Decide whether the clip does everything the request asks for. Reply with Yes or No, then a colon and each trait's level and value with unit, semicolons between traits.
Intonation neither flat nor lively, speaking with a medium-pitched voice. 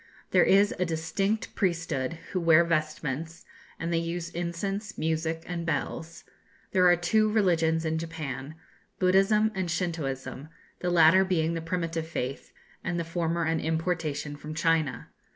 No: narrow, 1.9 semitones; medium, 165 Hz